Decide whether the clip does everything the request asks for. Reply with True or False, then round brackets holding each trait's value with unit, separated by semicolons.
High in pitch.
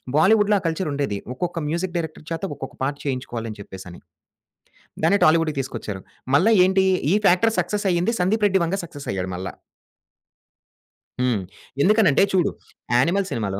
False (165 Hz)